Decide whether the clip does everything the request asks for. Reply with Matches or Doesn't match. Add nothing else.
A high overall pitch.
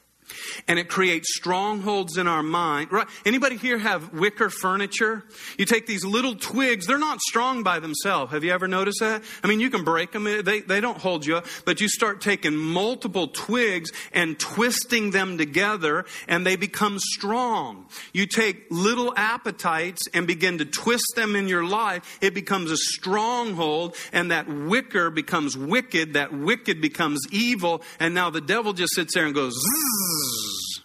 Matches